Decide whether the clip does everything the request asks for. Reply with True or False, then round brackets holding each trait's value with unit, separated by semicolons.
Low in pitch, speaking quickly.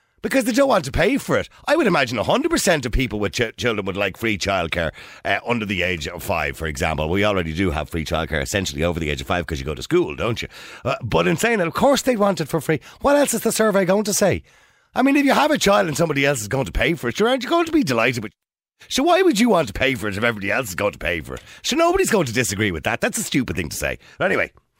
True (130 Hz; 305 wpm)